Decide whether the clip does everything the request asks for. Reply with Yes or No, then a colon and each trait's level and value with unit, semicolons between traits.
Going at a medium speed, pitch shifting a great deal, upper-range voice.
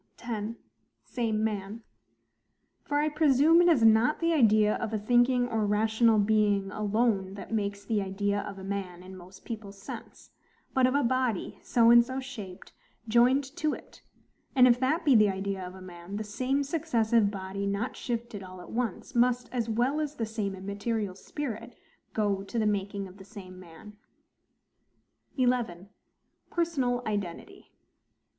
No: average, 165 wpm; average, 3.7 semitones; high, 220 Hz